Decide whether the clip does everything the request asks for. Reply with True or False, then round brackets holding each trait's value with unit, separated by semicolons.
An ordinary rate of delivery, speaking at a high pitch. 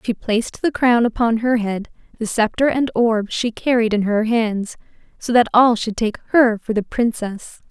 True (195 wpm; 225 Hz)